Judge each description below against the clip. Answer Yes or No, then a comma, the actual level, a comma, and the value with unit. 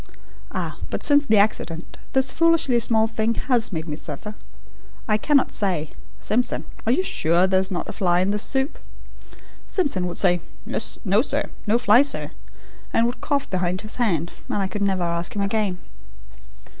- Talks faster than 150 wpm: Yes, average, 175 wpm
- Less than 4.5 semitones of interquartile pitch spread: No, average, 5.2 semitones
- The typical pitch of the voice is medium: No, high, 210 Hz